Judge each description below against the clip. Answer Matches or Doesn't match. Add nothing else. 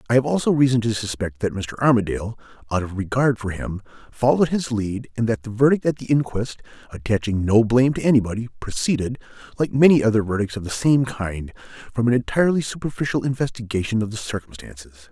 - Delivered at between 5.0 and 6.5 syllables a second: Matches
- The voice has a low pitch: Matches